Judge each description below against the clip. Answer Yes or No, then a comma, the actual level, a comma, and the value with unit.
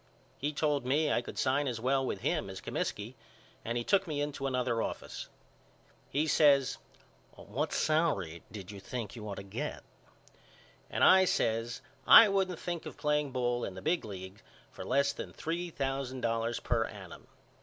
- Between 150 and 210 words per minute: Yes, average, 175 wpm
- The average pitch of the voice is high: No, low, 130 Hz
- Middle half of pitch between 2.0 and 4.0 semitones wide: No, average, 4.8 semitones